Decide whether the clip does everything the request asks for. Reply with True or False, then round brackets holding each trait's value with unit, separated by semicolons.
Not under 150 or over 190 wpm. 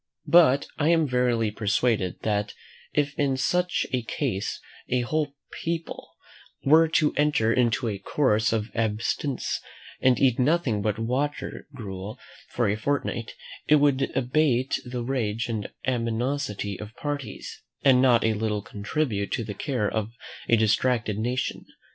False (140 wpm)